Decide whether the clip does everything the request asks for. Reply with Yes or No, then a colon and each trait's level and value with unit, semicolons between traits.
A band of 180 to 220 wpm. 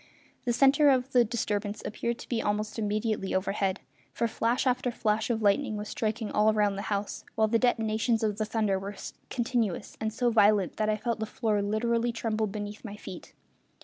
Yes: average, 190 wpm